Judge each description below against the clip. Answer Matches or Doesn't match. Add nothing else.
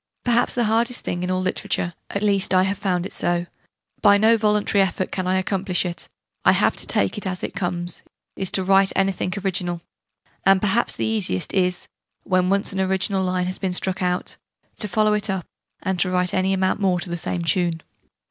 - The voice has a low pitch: Doesn't match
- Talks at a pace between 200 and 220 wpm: Matches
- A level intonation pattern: Matches